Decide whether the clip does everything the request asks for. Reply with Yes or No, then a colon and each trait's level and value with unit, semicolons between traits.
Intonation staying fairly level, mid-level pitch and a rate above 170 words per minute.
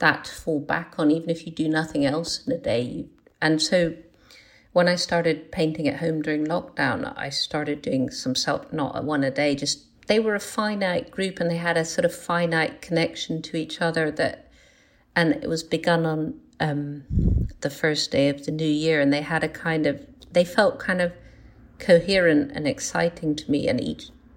Yes: narrow, 2.3 semitones; medium, 160 Hz; average, 200 wpm